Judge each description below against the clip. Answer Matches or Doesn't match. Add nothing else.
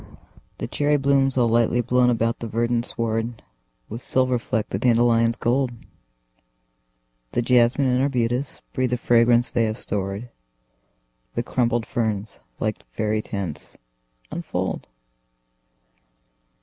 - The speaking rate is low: Matches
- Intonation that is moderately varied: Doesn't match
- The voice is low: Matches